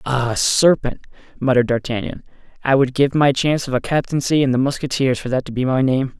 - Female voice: No, male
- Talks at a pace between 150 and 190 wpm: No, fast, 205 wpm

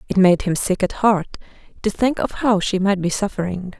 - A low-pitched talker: No, high, 195 Hz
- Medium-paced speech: No, fast, 220 wpm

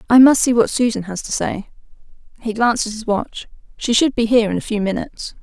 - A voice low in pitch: No, high, 225 Hz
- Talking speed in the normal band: No, fast, 230 wpm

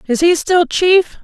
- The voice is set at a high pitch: Yes, very high, 335 Hz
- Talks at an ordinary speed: Yes, average, 195 wpm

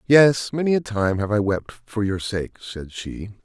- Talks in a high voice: No, low, 110 Hz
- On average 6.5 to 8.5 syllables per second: No, 4.6 syllables/s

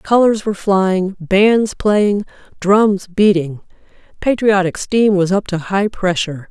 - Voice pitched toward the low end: No, high, 195 Hz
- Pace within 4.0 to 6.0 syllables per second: No, 3.8 syllables/s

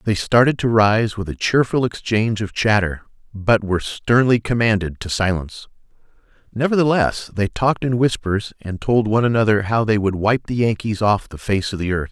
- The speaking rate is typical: Yes, average, 185 wpm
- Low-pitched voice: Yes, low, 110 Hz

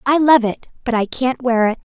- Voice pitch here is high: Yes, high, 245 Hz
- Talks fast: Yes, fast, 250 wpm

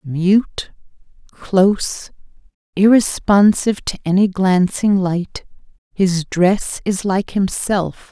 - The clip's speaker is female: Yes, female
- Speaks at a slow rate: Yes, slow, 90 wpm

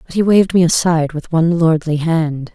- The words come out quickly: Yes, fast, 210 wpm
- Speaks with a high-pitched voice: No, medium, 165 Hz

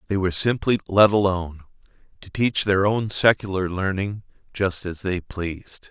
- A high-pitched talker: No, very low, 95 Hz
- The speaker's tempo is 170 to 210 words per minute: No, average, 150 wpm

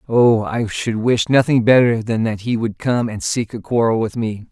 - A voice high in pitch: No, low, 115 Hz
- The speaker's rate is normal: No, fast, 225 wpm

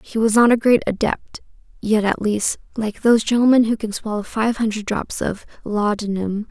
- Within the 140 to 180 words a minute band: No, average, 195 wpm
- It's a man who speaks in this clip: No, female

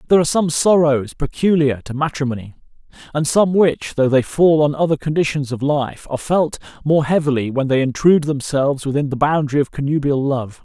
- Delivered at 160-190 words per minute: Yes, average, 180 wpm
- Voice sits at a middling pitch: Yes, medium, 145 Hz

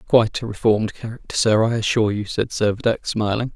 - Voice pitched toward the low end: Yes, low, 110 Hz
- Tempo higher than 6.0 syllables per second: Yes, 6.3 syllables/s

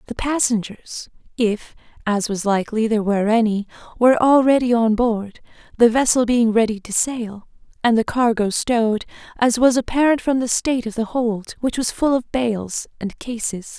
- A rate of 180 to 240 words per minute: No, average, 170 wpm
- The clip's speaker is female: Yes, female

